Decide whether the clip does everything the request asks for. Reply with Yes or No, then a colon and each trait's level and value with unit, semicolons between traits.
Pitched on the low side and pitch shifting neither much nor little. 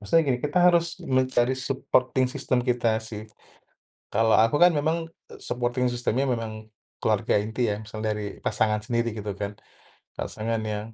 Yes: low, 120 Hz; average, 3.2 semitones